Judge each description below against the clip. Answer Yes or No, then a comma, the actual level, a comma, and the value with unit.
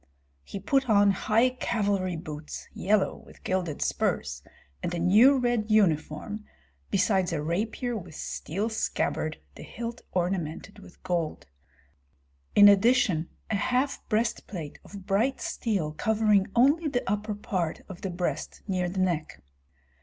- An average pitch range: Yes, average, 4.1 semitones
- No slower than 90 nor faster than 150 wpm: Yes, slow, 135 wpm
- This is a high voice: Yes, high, 200 Hz